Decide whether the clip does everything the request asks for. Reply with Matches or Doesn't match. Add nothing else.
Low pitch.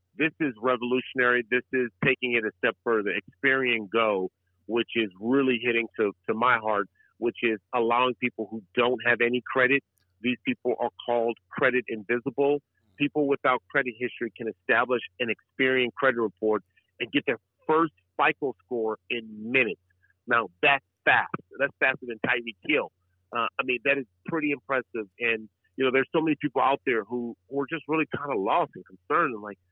Matches